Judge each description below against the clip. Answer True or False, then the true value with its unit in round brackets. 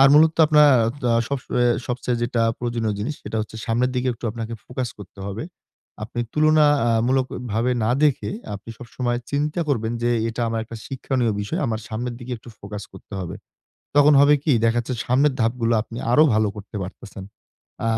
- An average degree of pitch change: True (3.0 semitones)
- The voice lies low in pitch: True (120 Hz)